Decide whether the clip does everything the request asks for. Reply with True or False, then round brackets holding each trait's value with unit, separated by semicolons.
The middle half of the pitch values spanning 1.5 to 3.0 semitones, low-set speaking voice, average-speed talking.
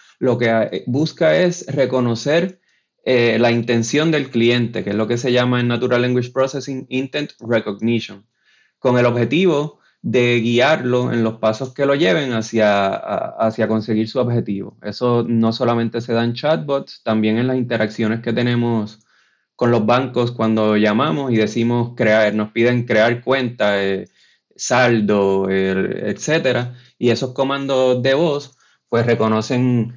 True (2.5 semitones; 120 Hz; 150 wpm)